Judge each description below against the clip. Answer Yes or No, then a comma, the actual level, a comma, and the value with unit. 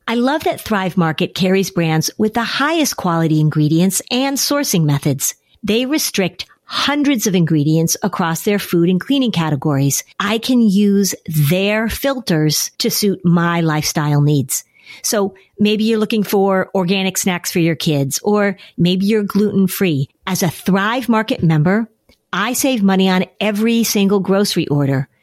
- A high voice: Yes, high, 195 Hz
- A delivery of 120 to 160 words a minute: Yes, average, 150 wpm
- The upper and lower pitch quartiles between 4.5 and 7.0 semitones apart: Yes, average, 4.8 semitones